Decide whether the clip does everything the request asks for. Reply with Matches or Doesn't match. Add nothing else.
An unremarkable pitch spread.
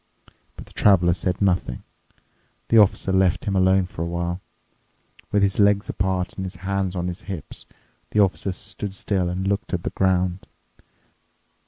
Doesn't match